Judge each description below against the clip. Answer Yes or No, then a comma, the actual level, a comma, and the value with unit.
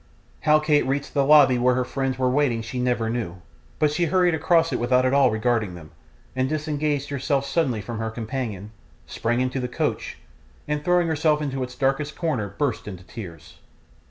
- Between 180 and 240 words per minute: Yes, average, 185 wpm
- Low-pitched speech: Yes, low, 130 Hz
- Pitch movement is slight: No, average, 3.9 semitones